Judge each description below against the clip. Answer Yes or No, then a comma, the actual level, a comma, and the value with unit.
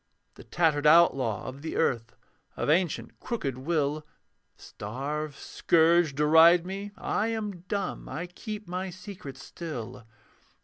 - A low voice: No, medium, 160 Hz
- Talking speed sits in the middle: No, slow, 125 wpm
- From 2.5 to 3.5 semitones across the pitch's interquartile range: No, average, 4.4 semitones